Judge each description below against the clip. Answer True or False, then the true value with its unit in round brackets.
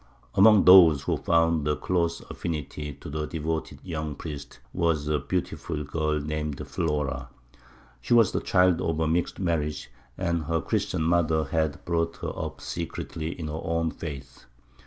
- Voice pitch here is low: True (80 Hz)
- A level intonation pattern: True (2.0 semitones)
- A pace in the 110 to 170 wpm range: True (155 wpm)